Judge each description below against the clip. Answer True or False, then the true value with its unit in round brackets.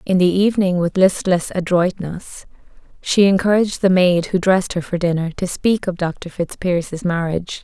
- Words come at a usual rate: True (165 wpm)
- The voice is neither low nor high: True (180 Hz)